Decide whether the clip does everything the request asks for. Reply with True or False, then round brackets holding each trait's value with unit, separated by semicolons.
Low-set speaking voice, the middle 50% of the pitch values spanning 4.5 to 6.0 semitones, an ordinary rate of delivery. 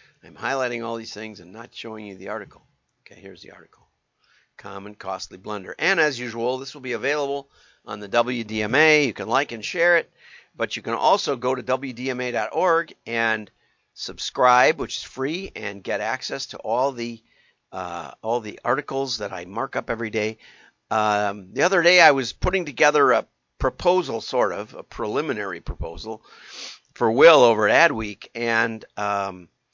False (115 Hz; 4.1 semitones; 170 wpm)